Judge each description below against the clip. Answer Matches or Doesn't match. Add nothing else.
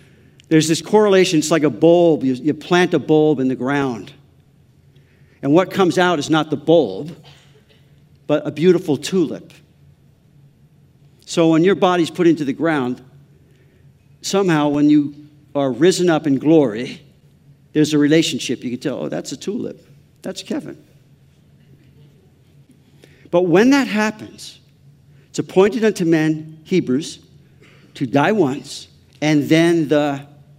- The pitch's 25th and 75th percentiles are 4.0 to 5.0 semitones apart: Doesn't match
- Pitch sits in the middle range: Matches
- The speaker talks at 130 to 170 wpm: Matches